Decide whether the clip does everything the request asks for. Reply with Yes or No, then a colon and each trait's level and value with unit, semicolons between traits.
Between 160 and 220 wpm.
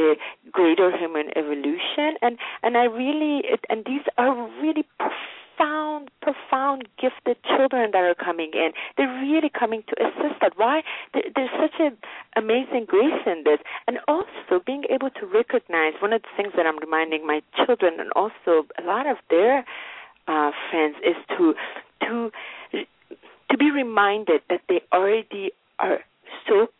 No: average, 150 wpm